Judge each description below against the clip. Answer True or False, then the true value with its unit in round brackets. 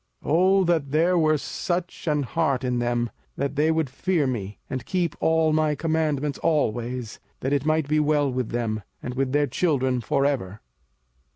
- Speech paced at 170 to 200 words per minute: True (180 wpm)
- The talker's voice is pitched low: False (145 Hz)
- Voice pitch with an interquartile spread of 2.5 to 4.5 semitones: True (3.9 semitones)